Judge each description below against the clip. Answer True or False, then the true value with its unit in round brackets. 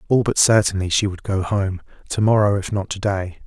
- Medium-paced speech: False (225 wpm)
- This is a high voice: False (100 Hz)